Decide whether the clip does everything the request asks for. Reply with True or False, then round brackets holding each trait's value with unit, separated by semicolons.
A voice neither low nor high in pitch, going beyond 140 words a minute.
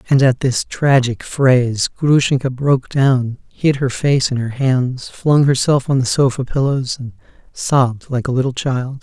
False (130 Hz; 175 wpm)